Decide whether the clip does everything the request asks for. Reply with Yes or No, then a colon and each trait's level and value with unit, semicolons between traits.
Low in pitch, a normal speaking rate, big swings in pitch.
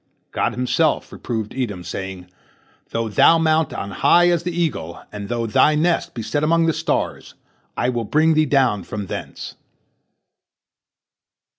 Yes: low, 130 Hz; average, 150 wpm; wide, 7.2 semitones